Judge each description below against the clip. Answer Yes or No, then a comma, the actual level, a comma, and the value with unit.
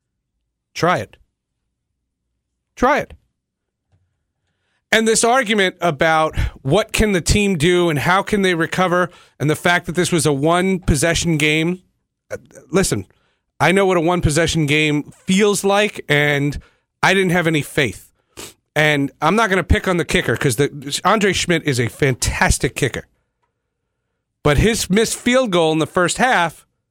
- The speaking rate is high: No, average, 155 wpm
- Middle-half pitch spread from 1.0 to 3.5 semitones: No, average, 4.5 semitones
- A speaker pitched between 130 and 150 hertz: No, medium, 170 Hz